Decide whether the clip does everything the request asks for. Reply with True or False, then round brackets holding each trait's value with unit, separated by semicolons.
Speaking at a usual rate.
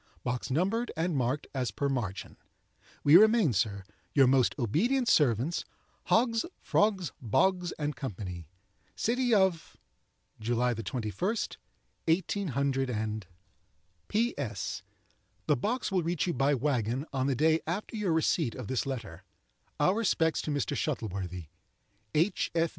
False (120 wpm)